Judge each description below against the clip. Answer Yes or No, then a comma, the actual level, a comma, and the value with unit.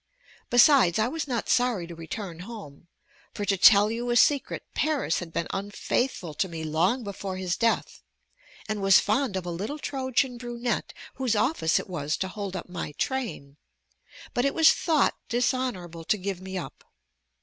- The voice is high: Yes, high, 205 Hz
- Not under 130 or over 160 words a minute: No, average, 170 wpm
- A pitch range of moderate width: No, wide, 5.7 semitones